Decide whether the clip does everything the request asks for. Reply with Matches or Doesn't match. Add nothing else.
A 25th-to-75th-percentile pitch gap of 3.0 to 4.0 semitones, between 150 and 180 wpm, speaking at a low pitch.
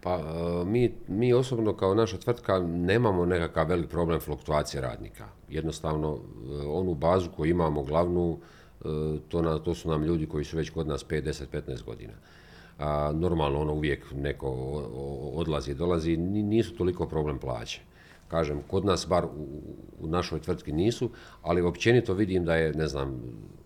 Matches